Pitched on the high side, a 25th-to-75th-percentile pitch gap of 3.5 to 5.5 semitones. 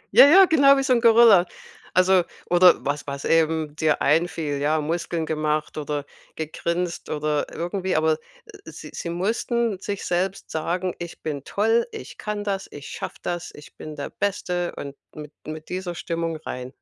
No: medium, 170 Hz; average, 4.0 semitones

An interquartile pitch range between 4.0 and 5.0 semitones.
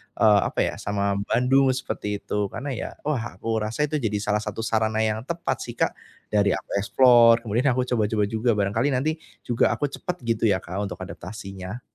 No: average, 3.4 semitones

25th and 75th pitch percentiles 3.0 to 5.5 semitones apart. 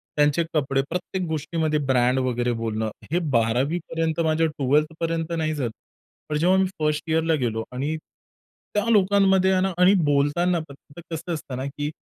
Yes: average, 3.9 semitones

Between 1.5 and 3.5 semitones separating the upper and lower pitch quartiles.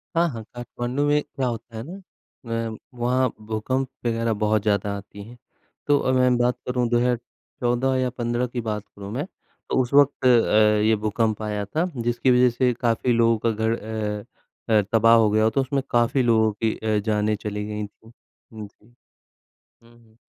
Yes: narrow, 2.5 semitones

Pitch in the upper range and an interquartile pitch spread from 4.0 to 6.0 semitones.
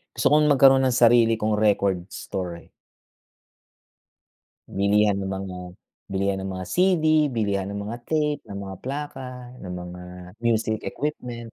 No: low, 110 Hz; average, 5.3 semitones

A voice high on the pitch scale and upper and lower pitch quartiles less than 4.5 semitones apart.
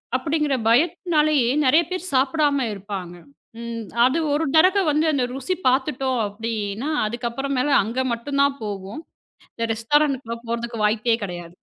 No: very high, 260 Hz; average, 4.8 semitones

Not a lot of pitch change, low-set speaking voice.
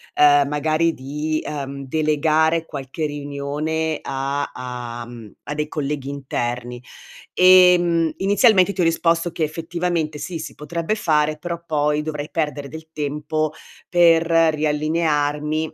No: narrow, 2.3 semitones; medium, 155 Hz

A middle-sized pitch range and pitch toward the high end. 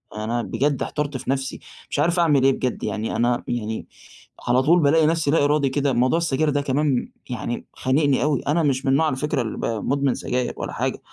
No: average, 3.0 semitones; low, 135 Hz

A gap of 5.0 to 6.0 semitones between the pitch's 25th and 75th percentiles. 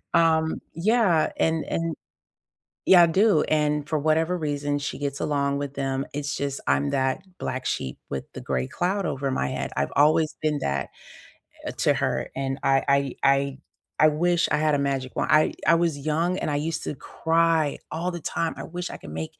No: average, 3.1 semitones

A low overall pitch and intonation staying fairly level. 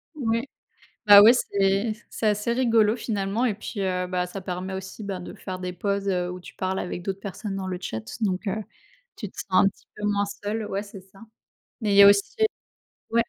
No: high, 200 Hz; narrow, 2.2 semitones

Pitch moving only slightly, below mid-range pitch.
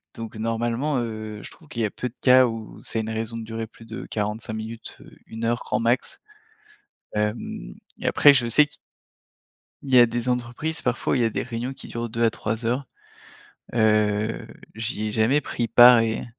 Yes: narrow, 1.9 semitones; low, 115 Hz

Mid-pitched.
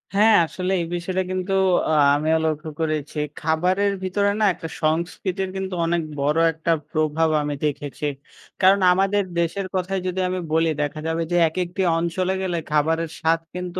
Yes: medium, 170 Hz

